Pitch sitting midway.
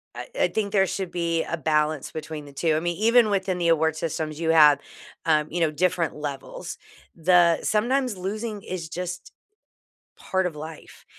Yes: medium, 170 Hz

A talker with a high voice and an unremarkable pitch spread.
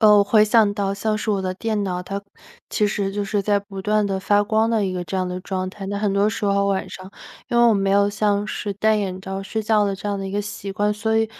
No: high, 205 Hz; narrow, 1.4 semitones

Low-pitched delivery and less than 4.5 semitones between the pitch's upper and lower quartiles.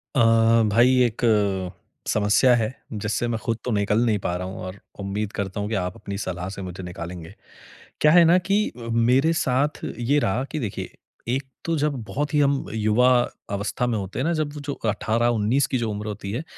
No: low, 115 Hz; average, 4.9 semitones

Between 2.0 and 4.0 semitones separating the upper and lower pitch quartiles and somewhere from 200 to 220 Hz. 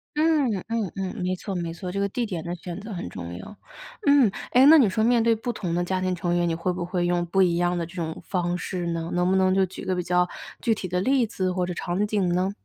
No: average, 3.1 semitones; medium, 185 Hz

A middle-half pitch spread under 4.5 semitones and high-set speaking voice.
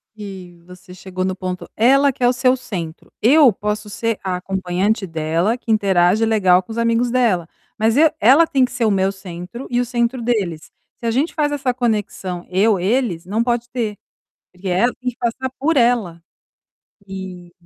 No: average, 4.8 semitones; high, 215 Hz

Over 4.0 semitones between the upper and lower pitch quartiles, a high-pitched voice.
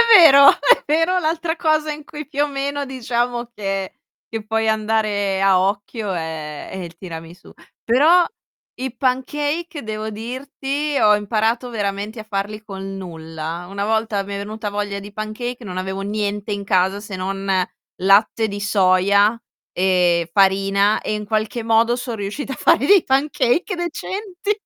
Yes: average, 5.0 semitones; high, 215 Hz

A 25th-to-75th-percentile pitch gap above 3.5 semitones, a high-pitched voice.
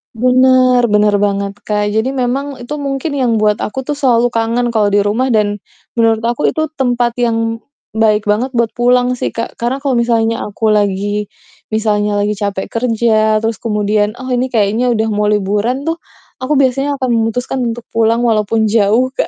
No: average, 3.0 semitones; high, 230 Hz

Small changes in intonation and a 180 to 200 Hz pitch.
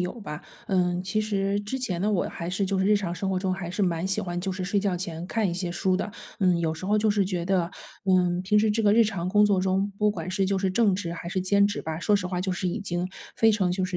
Yes: narrow, 2.3 semitones; high, 190 Hz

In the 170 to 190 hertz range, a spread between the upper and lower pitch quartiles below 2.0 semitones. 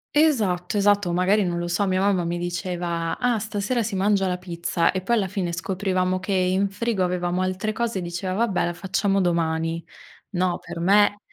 No: medium, 185 Hz; narrow, 2.5 semitones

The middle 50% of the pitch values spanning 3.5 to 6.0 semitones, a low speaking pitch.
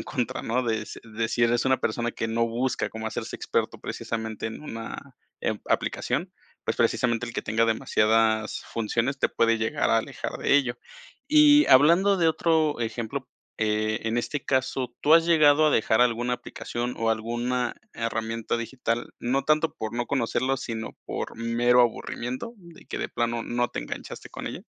No: average, 2.9 semitones; low, 120 Hz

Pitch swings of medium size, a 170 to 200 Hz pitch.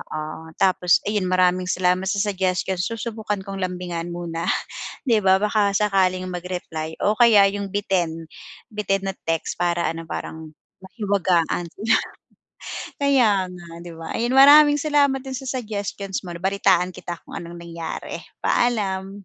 Yes: average, 3.2 semitones; high, 190 Hz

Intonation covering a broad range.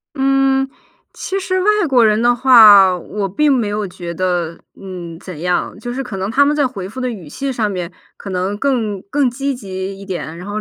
Yes: wide, 6.1 semitones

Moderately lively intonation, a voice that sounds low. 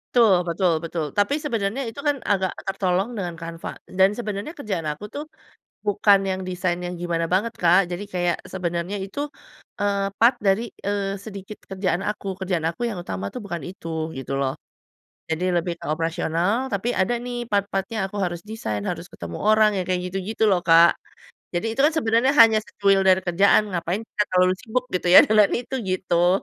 No: average, 3.5 semitones; high, 195 Hz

